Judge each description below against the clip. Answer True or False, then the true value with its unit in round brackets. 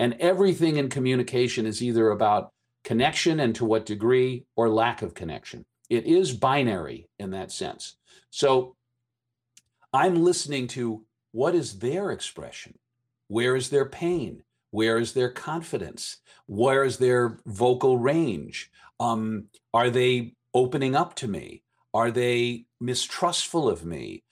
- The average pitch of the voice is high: False (120 Hz)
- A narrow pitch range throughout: True (2.0 semitones)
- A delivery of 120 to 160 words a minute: True (135 wpm)